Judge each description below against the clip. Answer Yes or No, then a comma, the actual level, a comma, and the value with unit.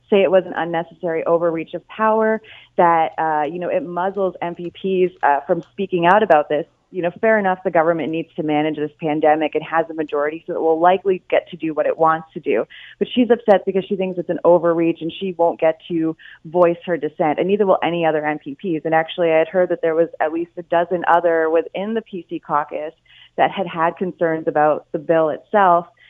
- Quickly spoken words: Yes, fast, 220 wpm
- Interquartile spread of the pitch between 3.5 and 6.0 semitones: No, narrow, 2.4 semitones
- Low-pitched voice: No, medium, 170 Hz